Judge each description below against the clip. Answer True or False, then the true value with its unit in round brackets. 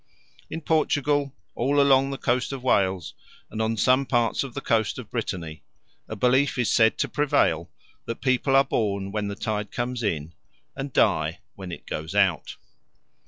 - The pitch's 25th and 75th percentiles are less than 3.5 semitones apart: False (5.1 semitones)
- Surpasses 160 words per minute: True (170 wpm)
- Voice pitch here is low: True (120 Hz)